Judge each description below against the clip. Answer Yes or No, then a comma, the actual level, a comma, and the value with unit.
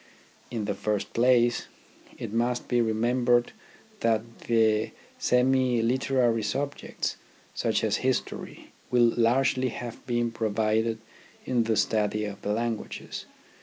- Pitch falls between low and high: No, low, 115 Hz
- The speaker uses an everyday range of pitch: No, narrow, 1.8 semitones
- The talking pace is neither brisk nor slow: No, slow, 120 wpm